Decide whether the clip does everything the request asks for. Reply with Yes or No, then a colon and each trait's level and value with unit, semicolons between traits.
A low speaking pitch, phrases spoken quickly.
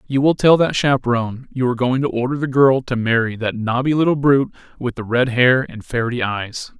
Yes: low, 125 Hz; fast, 220 wpm